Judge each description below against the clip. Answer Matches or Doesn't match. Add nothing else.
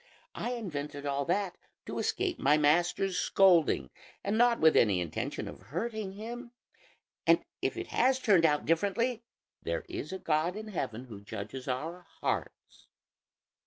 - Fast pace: Doesn't match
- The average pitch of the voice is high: Doesn't match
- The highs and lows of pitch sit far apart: Matches